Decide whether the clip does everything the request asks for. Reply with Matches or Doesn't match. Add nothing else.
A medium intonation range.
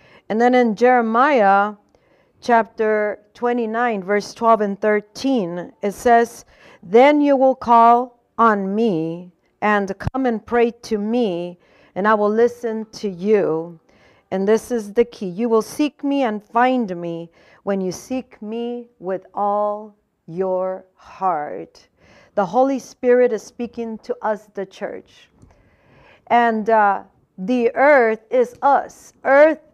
Matches